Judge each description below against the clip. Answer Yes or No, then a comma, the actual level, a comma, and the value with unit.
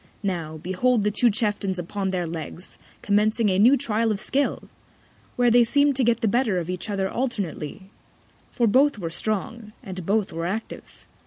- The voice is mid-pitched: No, high, 210 Hz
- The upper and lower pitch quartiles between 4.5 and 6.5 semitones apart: No, average, 4.1 semitones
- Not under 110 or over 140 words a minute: No, average, 175 wpm